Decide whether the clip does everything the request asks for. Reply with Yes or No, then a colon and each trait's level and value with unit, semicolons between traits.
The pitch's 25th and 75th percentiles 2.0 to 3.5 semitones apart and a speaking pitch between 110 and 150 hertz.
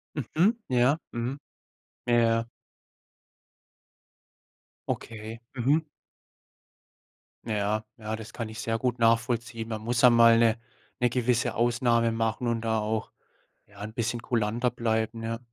No: narrow, 1.3 semitones; low, 115 Hz